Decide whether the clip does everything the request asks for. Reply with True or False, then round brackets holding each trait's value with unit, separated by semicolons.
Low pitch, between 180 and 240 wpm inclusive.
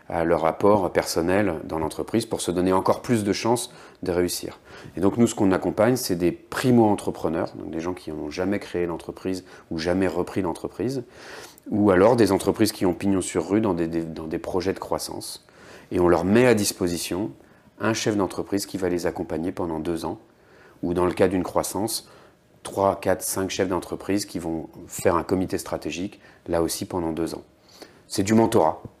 True (90 Hz; 195 wpm)